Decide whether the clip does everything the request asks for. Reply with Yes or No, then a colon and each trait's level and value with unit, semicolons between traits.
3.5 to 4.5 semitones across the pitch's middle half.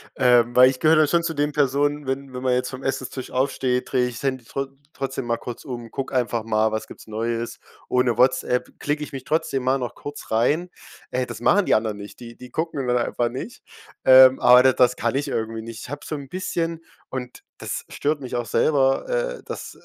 No: average, 2.9 semitones